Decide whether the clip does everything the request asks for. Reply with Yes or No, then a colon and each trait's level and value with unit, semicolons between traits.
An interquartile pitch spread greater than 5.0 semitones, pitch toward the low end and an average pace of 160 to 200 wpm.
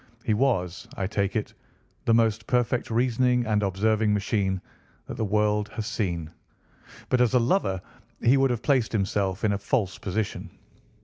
No: average, 3.1 semitones; low, 110 Hz; average, 165 wpm